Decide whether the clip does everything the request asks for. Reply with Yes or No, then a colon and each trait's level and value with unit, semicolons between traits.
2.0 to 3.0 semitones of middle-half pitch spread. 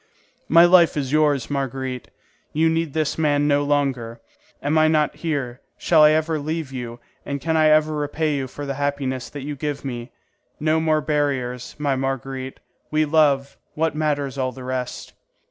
Yes: narrow, 2.6 semitones